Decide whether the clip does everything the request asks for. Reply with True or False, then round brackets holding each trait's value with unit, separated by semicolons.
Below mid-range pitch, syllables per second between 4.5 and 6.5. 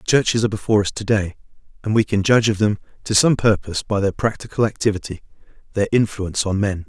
False (105 Hz; 6.8 syllables/s)